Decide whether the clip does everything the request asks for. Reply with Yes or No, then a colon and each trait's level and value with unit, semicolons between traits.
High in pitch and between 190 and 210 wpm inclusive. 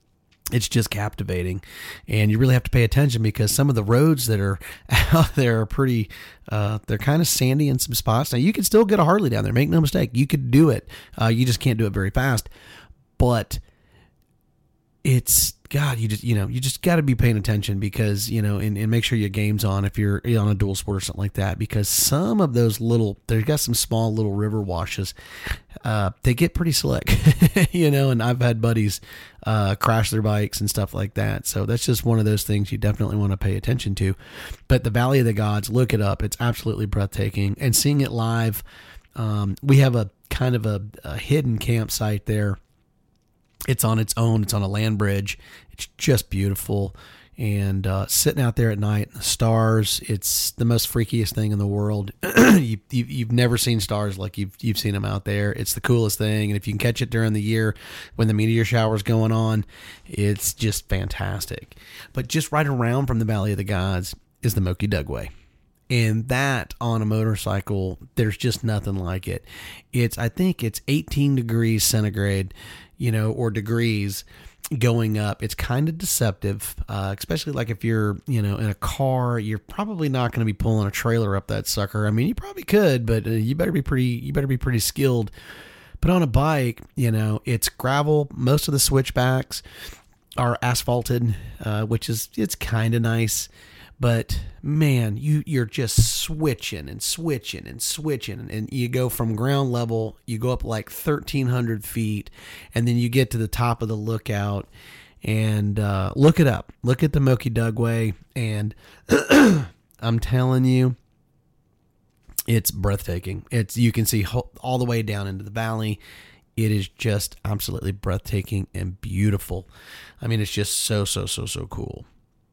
No: low, 110 Hz; average, 195 wpm